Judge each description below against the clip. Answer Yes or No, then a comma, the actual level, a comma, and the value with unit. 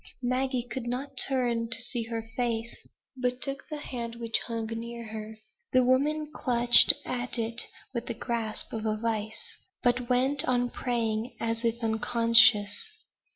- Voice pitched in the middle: No, high, 235 Hz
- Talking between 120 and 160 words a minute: Yes, average, 155 wpm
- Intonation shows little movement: Yes, narrow, 1.8 semitones